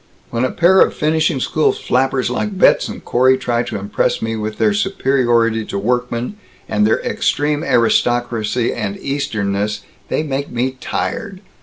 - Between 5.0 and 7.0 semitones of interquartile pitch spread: No, average, 4.4 semitones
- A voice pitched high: No, low, 125 Hz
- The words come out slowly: No, average, 155 wpm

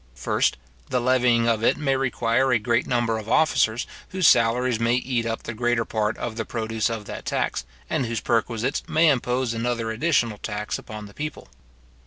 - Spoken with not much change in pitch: Yes, narrow, 2.1 semitones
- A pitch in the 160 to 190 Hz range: No, low, 115 Hz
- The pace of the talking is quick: No, average, 185 wpm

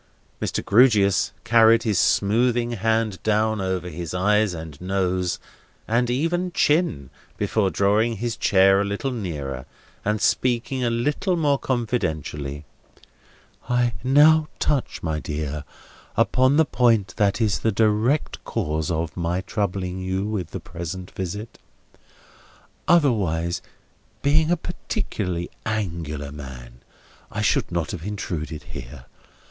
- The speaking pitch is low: Yes, low, 100 Hz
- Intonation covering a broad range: Yes, wide, 5.7 semitones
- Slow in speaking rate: Yes, slow, 125 wpm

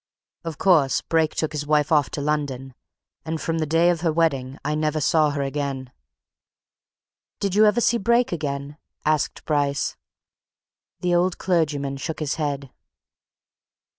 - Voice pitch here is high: No, medium, 150 Hz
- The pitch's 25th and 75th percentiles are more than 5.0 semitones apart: No, narrow, 2.6 semitones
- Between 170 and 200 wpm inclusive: No, average, 150 wpm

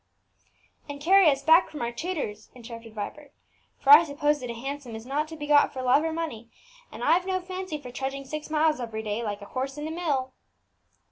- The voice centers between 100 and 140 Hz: No, very high, 285 Hz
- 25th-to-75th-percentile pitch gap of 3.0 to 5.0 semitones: Yes, average, 4.6 semitones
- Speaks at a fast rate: Yes, fast, 215 wpm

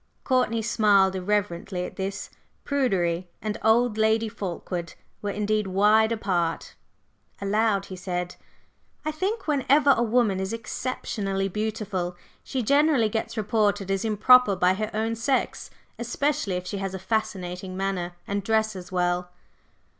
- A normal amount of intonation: Yes, average, 3.2 semitones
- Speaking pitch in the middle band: No, high, 210 Hz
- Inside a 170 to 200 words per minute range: No, slow, 135 wpm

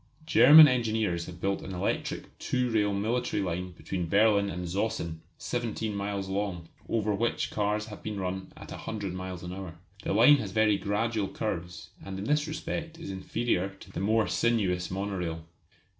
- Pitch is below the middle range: Yes, low, 100 Hz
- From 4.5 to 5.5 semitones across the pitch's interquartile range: No, average, 3.4 semitones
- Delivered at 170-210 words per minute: Yes, average, 175 wpm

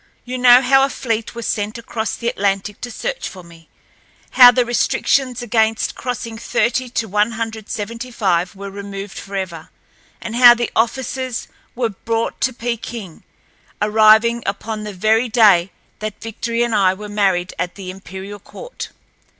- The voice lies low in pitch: No, high, 220 Hz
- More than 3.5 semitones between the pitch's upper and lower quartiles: No, average, 3.1 semitones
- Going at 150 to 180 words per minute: Yes, average, 160 wpm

